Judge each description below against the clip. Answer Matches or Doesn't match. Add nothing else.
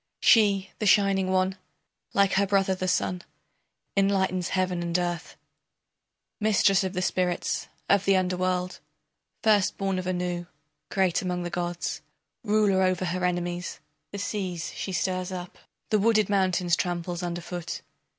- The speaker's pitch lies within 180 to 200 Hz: Matches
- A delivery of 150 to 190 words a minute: Doesn't match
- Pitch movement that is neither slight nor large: Doesn't match